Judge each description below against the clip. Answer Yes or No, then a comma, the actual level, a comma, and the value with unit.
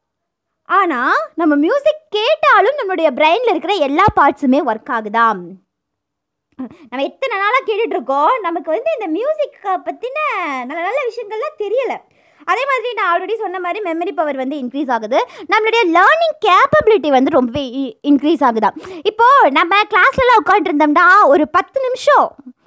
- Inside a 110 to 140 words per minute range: Yes, fast, 130 wpm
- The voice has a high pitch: Yes, very high, 345 Hz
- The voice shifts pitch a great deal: Yes, wide, 5.9 semitones